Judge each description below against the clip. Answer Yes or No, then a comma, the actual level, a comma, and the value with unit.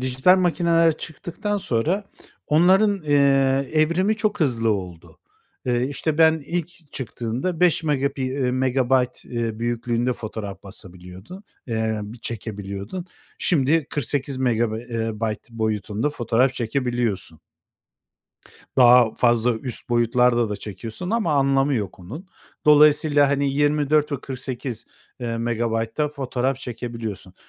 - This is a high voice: No, low, 130 Hz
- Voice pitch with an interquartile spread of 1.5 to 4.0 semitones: No, average, 4.7 semitones